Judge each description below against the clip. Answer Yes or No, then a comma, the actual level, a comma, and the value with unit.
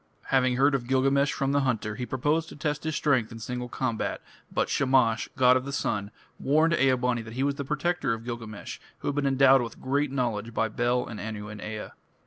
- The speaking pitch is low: Yes, low, 130 Hz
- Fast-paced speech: Yes, fast, 220 wpm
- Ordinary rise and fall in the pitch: Yes, average, 3.4 semitones